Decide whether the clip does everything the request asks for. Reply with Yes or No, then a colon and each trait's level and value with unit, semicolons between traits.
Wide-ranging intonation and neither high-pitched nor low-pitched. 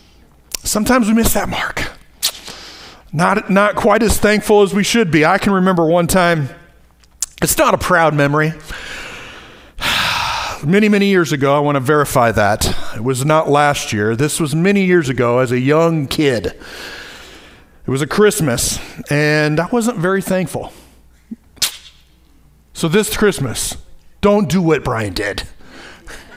Yes: wide, 7.5 semitones; medium, 155 Hz